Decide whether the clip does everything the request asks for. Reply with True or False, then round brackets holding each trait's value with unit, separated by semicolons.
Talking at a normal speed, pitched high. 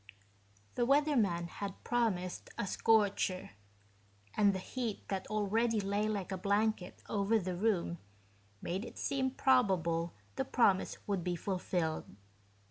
False (130 wpm; 200 Hz)